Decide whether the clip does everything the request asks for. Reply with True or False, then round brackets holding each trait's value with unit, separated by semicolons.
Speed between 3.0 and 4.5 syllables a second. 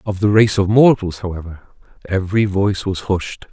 False (5.3 syllables/s)